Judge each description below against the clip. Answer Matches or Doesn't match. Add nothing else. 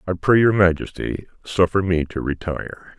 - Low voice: Matches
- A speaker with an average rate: Matches